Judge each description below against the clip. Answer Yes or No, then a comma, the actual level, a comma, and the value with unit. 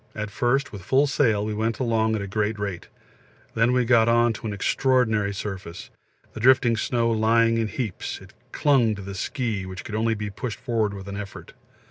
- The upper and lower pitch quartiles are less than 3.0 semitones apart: Yes, narrow, 2.5 semitones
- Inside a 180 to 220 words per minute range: Yes, average, 200 wpm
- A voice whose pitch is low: Yes, low, 110 Hz